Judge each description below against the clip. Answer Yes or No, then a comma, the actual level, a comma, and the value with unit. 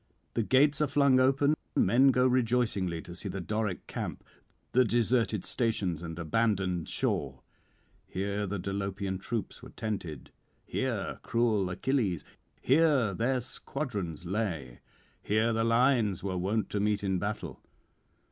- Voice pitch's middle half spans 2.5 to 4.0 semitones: No, average, 4.8 semitones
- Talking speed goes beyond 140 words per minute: No, slow, 135 wpm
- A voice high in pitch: No, low, 105 Hz